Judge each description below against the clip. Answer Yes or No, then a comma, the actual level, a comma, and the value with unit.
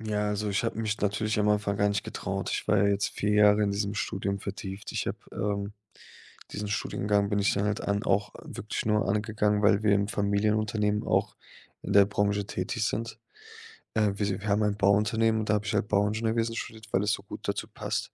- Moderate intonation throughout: No, narrow, 1.0 semitones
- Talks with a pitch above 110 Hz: No, low, 105 Hz